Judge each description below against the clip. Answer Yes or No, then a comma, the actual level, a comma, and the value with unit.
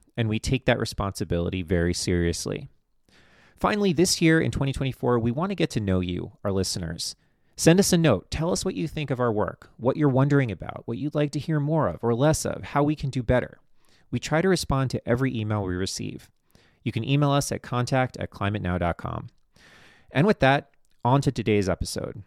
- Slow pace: No, average, 200 wpm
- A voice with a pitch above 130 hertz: No, low, 125 Hz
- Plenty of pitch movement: Yes, wide, 5.8 semitones